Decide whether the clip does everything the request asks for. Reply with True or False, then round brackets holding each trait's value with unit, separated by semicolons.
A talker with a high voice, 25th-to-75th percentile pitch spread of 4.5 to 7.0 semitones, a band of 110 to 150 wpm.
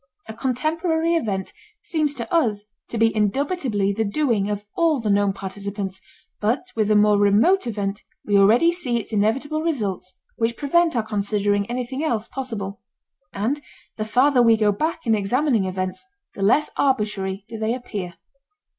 False (220 Hz; 5.0 semitones; 160 wpm)